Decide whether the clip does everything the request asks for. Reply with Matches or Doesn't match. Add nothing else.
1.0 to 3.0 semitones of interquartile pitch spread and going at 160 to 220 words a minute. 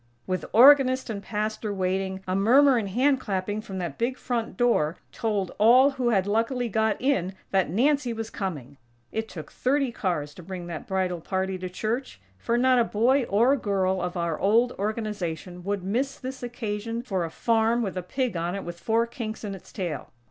Doesn't match